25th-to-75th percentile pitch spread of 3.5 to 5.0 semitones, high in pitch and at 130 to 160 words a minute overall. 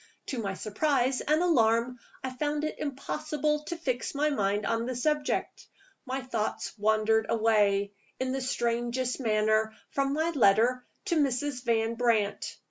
Yes: average, 4.3 semitones; very high, 250 Hz; average, 145 wpm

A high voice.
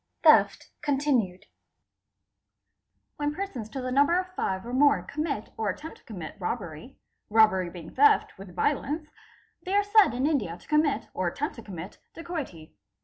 Yes: very high, 260 Hz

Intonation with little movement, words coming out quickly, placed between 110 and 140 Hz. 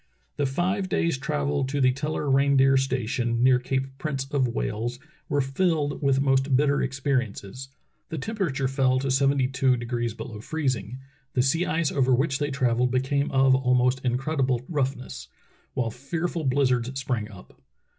No: narrow, 2.0 semitones; average, 165 wpm; low, 135 Hz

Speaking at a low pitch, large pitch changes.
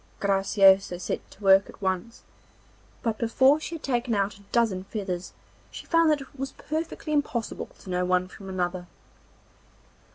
No: high, 205 Hz; wide, 5.8 semitones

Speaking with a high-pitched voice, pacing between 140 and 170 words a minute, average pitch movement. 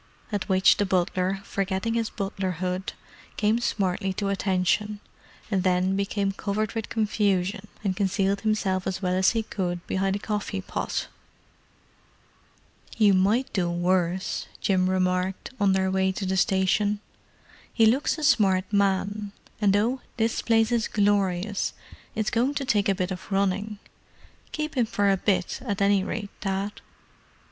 No: high, 195 Hz; average, 150 wpm; narrow, 2.0 semitones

